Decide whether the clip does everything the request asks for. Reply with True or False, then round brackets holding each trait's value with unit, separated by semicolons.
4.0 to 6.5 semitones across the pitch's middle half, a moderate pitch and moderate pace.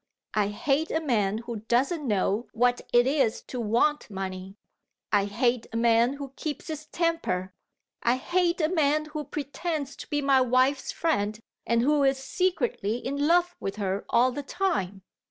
False (5.6 semitones; 260 Hz; 170 wpm)